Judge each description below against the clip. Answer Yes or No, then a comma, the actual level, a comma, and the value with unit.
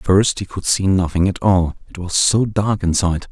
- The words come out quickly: Yes, fast, 235 wpm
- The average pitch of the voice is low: Yes, very low, 95 Hz